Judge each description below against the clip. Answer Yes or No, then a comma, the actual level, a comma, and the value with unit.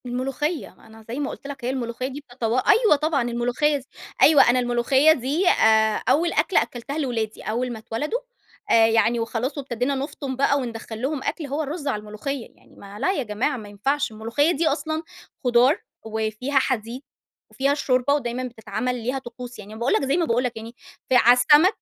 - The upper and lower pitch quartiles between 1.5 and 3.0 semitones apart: No, average, 3.7 semitones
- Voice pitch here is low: No, very high, 250 Hz